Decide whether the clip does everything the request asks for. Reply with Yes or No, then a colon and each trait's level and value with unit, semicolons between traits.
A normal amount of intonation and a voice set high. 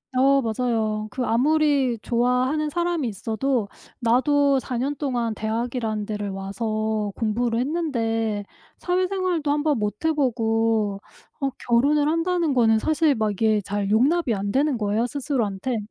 Yes: average, 4.9 semitones; high, 240 Hz